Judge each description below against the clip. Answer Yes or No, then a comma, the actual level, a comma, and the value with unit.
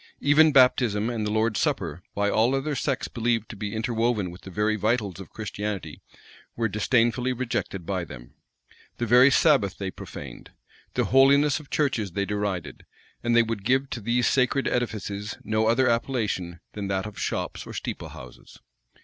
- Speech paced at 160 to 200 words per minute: Yes, average, 165 wpm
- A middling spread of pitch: Yes, average, 3.7 semitones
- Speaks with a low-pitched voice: Yes, low, 110 Hz